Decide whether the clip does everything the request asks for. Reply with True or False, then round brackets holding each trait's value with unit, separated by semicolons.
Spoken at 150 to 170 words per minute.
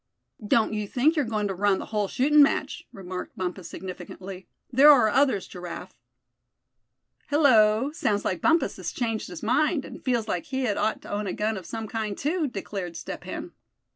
False (185 wpm)